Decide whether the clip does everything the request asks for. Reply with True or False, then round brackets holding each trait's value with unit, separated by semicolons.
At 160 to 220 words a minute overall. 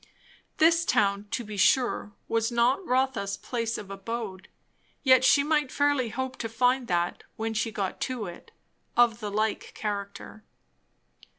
False (150 wpm)